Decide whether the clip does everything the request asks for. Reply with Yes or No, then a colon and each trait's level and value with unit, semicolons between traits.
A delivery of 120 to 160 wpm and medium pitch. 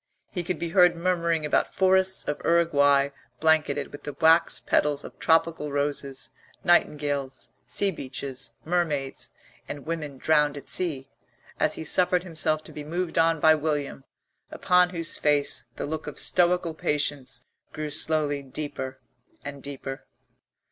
Yes: average, 140 wpm; medium, 155 Hz